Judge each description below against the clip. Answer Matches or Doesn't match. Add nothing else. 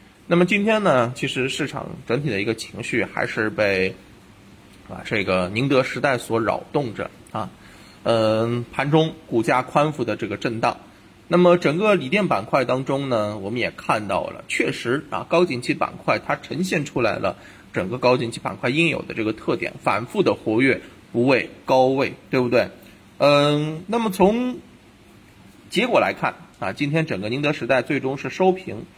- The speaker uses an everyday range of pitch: Doesn't match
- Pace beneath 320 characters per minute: Matches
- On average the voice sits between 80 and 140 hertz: Matches